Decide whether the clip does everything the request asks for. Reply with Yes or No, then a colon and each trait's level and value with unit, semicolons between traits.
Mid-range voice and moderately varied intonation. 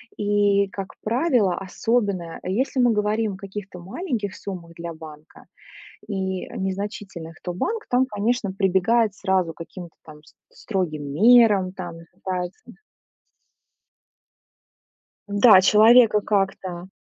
No: high, 195 Hz; average, 3.0 semitones